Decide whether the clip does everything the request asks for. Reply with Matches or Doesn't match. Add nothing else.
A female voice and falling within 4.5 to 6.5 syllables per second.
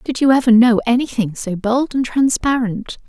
Matches